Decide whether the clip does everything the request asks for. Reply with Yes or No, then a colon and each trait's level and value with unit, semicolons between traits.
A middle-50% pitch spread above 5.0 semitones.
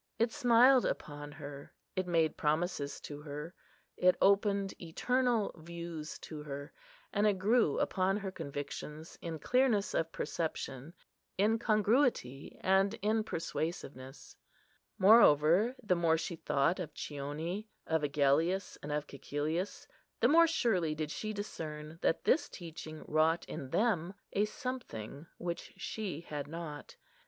Yes: wide, 5.5 semitones